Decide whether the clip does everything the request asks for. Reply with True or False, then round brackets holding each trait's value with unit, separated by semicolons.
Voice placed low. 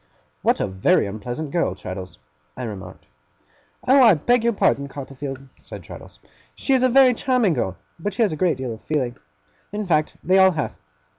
False (155 Hz)